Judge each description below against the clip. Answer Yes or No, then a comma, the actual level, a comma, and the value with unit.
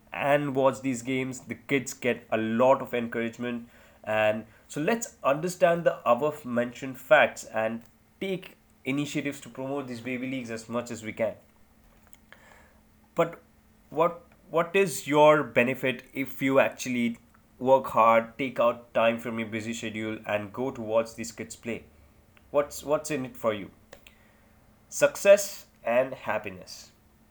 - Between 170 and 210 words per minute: No, average, 145 wpm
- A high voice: No, low, 125 Hz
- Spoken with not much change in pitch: No, average, 3.7 semitones